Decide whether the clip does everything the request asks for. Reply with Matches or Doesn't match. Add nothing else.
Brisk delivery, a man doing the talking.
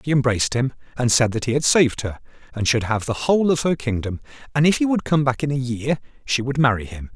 Matches